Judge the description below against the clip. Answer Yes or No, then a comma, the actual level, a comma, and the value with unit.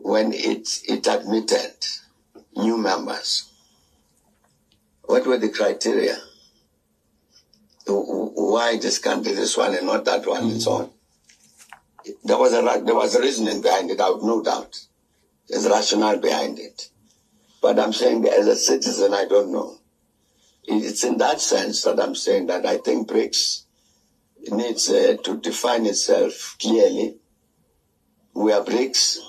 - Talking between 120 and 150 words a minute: Yes, slow, 135 wpm